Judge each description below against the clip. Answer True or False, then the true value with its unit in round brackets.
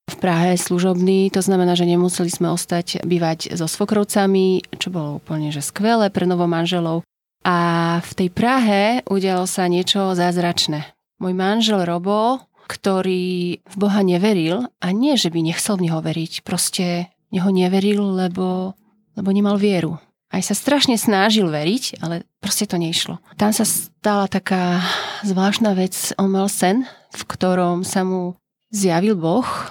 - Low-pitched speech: False (185 Hz)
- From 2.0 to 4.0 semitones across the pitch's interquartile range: True (2.6 semitones)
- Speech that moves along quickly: False (150 wpm)